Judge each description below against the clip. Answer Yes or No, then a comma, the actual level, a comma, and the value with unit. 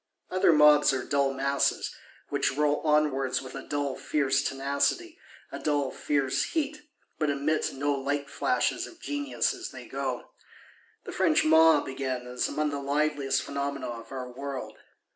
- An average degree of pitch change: No, narrow, 2.1 semitones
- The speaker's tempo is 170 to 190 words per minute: No, average, 155 wpm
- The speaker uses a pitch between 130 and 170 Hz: Yes, medium, 140 Hz